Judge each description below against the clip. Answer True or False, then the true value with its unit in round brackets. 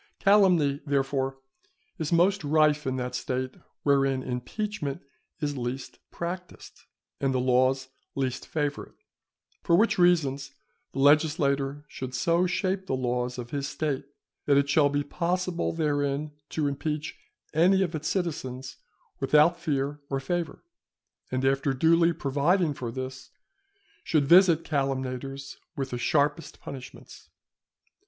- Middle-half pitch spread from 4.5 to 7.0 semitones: False (3.6 semitones)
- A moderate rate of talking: False (130 wpm)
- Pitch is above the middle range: False (145 Hz)